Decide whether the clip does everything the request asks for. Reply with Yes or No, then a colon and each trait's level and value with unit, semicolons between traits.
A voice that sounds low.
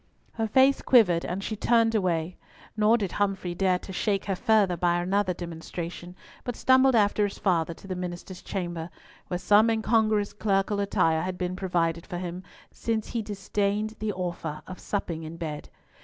No: high, 190 Hz